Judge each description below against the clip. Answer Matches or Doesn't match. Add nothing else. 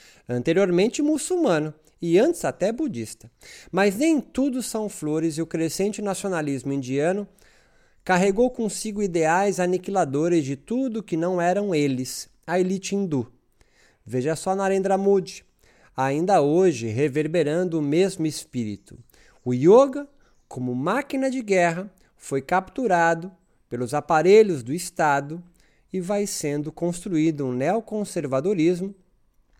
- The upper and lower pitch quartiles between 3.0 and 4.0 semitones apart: Doesn't match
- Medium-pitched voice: Matches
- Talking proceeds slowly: Matches